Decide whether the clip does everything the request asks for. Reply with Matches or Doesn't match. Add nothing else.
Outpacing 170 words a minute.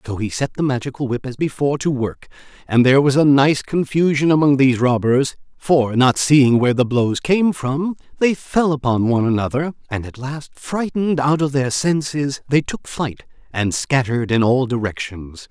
Matches